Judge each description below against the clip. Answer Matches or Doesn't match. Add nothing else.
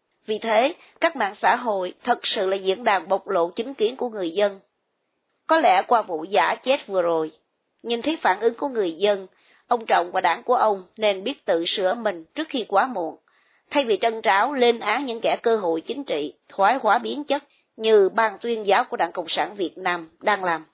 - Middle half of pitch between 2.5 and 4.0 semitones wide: Doesn't match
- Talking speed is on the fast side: Doesn't match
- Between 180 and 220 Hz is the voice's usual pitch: Matches